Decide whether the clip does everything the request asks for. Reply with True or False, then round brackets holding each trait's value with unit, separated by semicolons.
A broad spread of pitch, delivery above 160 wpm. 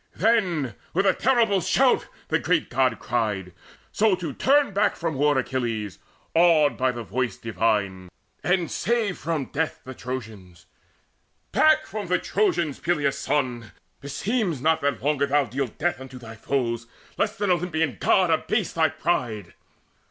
False (6.4 semitones; 150 wpm)